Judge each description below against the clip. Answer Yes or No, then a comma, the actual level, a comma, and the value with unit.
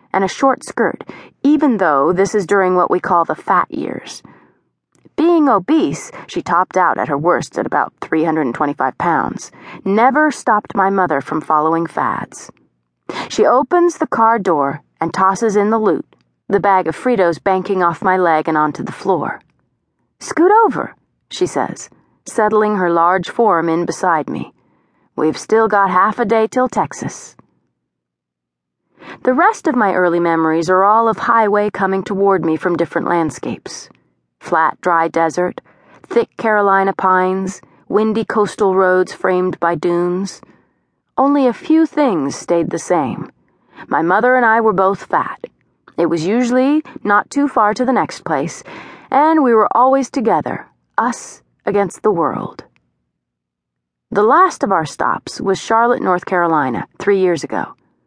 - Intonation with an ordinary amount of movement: No, wide, 5.9 semitones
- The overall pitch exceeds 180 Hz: Yes, high, 190 Hz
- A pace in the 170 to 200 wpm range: No, average, 155 wpm